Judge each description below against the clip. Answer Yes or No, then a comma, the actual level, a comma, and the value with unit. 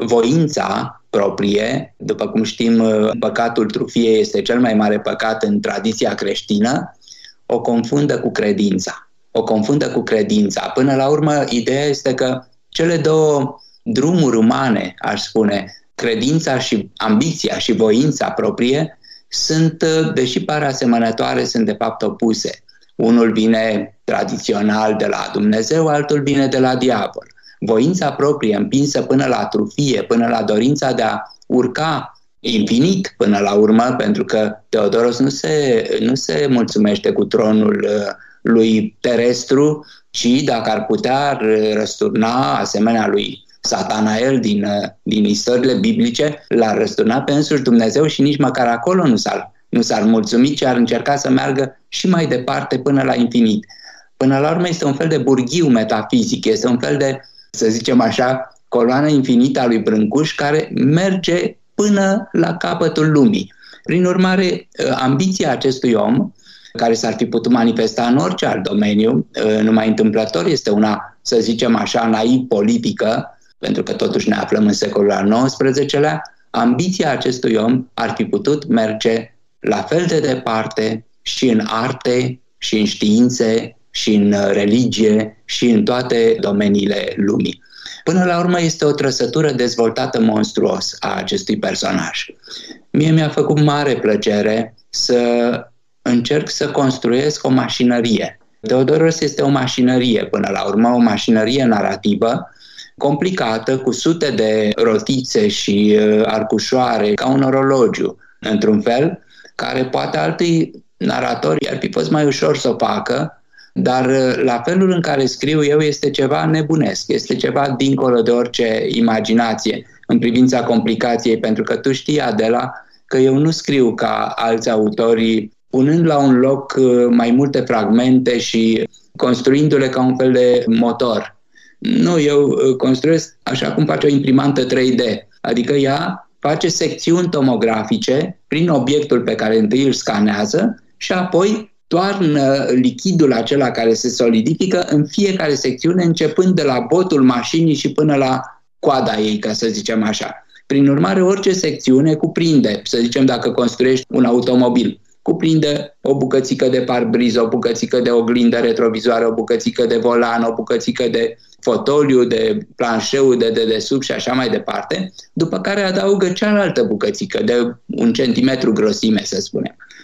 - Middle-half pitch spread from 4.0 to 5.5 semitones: Yes, average, 4.7 semitones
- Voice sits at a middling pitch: No, low, 130 Hz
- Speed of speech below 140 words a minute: No, average, 145 wpm